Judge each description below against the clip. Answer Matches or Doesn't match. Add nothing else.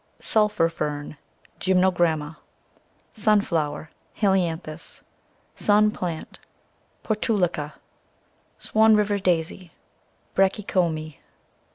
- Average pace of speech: Doesn't match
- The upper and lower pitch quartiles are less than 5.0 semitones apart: Matches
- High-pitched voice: Doesn't match